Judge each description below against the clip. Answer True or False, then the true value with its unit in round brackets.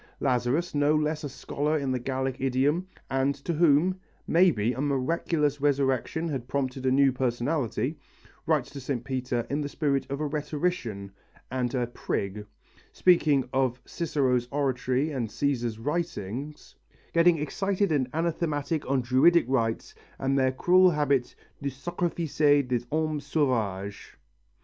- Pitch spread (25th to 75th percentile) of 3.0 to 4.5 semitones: True (3.3 semitones)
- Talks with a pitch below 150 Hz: True (140 Hz)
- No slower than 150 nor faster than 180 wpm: False (140 wpm)